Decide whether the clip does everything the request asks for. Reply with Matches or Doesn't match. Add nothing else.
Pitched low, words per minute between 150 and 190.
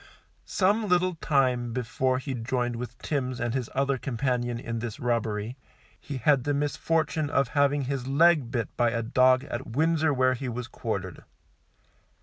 Matches